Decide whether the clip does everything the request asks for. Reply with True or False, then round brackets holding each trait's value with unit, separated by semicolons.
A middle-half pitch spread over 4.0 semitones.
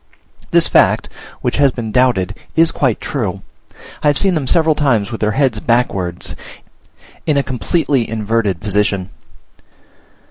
True (5.1 semitones)